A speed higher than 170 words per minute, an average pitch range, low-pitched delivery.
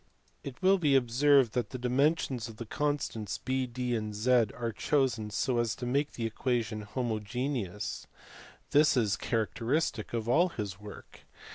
No: average, 155 wpm; average, 3.5 semitones; low, 120 Hz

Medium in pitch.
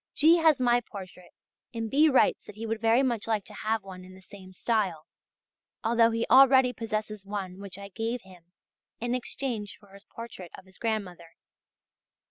No: high, 220 Hz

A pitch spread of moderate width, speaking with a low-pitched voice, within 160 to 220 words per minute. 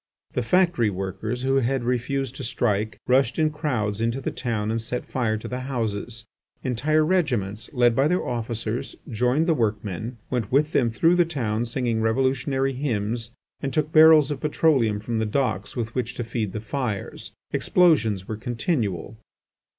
Yes: average, 3.7 semitones; low, 120 Hz; average, 165 wpm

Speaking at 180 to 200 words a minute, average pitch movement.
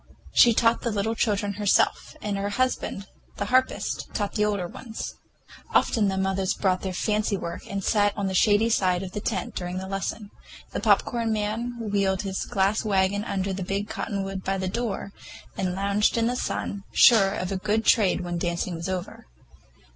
No: average, 190 wpm; narrow, 2.0 semitones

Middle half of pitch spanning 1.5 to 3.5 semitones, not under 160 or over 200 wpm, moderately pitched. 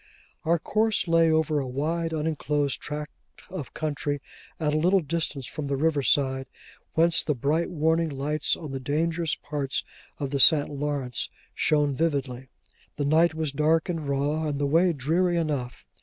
Yes: narrow, 2.6 semitones; average, 165 wpm; medium, 150 Hz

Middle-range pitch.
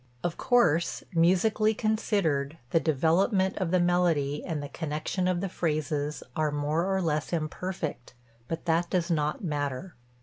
Yes: medium, 165 Hz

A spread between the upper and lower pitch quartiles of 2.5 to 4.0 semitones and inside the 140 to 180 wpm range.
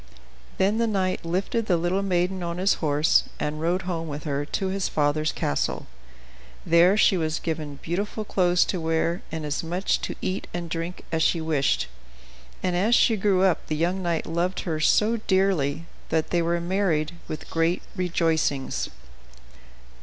Yes: average, 2.9 semitones; average, 170 wpm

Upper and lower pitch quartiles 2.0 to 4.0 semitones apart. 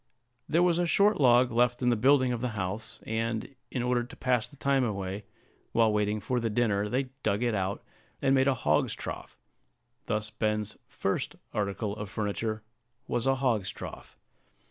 Yes: average, 3.3 semitones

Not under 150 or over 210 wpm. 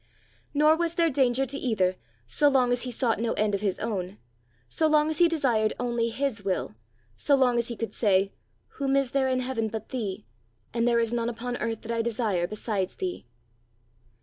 Yes: average, 200 wpm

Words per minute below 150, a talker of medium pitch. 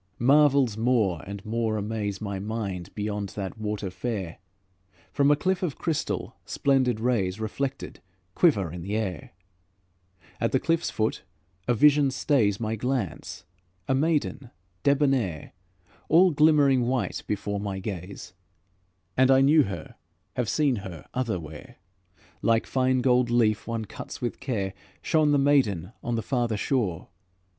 No: average, 140 wpm; low, 115 Hz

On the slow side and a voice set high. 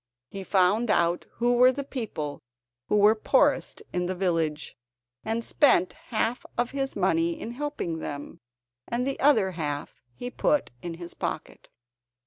No: average, 150 wpm; high, 205 Hz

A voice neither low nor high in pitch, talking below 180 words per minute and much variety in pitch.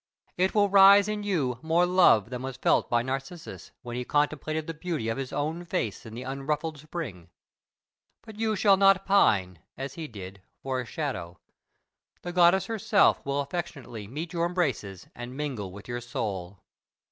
Yes: medium, 145 Hz; average, 170 wpm; wide, 6.7 semitones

